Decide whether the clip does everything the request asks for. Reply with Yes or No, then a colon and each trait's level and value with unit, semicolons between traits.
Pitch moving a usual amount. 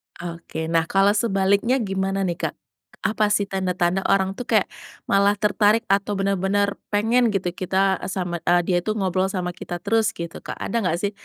No: narrow, 2.0 semitones